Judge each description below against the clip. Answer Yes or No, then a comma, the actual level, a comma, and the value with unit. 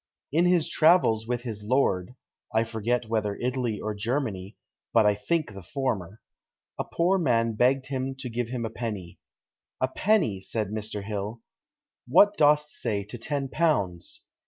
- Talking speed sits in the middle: Yes, average, 160 wpm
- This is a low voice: Yes, low, 115 Hz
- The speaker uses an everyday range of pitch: Yes, average, 4.4 semitones